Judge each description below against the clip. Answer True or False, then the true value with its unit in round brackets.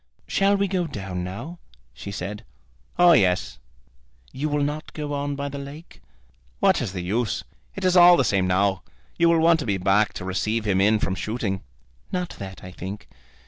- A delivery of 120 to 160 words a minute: False (190 wpm)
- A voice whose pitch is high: False (110 Hz)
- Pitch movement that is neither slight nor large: False (8.7 semitones)